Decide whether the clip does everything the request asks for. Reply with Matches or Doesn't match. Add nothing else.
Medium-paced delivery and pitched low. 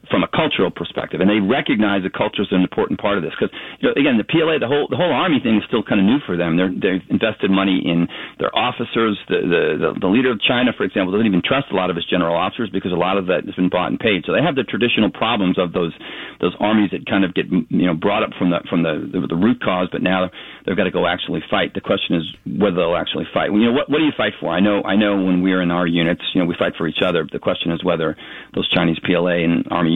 Doesn't match